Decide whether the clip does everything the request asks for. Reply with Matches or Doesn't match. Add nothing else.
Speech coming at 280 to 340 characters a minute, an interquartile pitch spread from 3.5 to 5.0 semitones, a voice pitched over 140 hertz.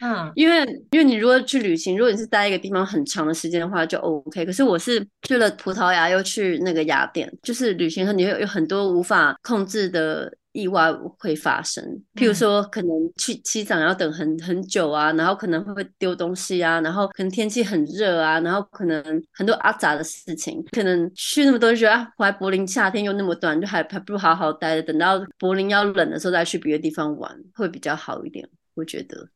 Matches